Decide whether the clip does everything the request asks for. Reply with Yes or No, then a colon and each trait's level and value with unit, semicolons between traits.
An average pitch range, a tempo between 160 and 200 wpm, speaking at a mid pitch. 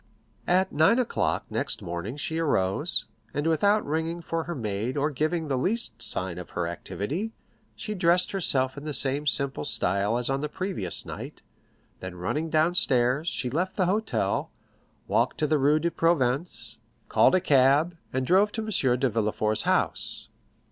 No: wide, 6.0 semitones; average, 165 wpm; medium, 145 Hz